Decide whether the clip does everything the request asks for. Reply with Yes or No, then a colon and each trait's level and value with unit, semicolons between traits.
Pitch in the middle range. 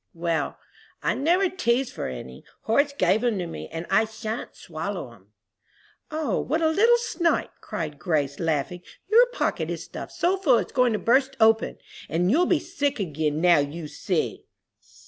No: high, 220 Hz